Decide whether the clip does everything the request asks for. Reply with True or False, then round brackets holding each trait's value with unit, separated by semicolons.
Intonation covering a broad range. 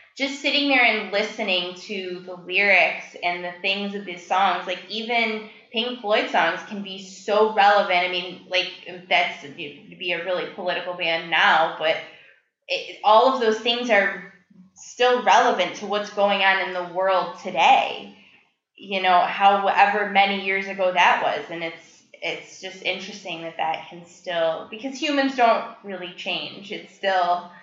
False (2.8 semitones)